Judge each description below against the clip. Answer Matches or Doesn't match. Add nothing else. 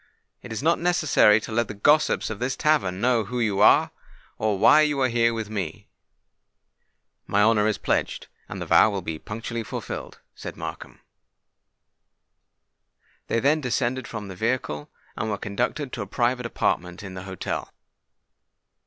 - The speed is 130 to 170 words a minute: Matches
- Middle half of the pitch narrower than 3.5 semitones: Doesn't match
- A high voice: Doesn't match